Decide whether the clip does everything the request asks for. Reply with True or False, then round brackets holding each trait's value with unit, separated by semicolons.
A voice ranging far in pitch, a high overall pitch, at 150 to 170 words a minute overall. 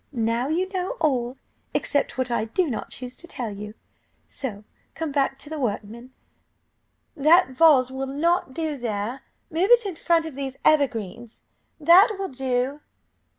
False (4.8 semitones; 270 Hz; 155 wpm)